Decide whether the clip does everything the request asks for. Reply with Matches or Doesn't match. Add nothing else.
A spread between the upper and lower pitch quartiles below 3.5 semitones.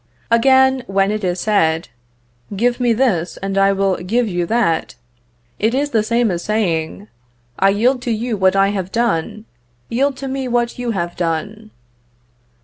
Doesn't match